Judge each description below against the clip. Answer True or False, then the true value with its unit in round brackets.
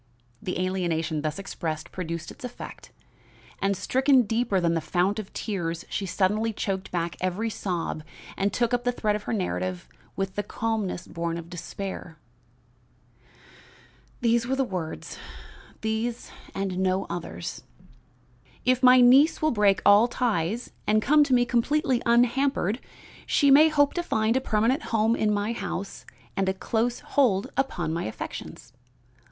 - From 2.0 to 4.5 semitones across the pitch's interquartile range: False (4.9 semitones)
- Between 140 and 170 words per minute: True (150 wpm)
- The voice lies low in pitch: False (205 Hz)